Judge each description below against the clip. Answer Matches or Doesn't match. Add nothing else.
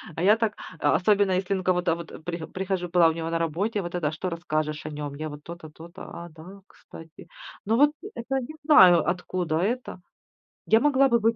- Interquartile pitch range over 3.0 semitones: Matches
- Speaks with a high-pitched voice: Doesn't match